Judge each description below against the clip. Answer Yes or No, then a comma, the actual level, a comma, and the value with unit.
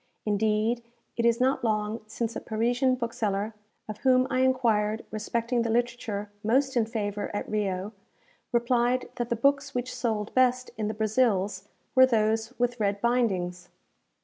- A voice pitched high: Yes, high, 230 Hz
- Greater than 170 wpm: No, average, 150 wpm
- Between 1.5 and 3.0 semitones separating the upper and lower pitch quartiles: Yes, narrow, 2.6 semitones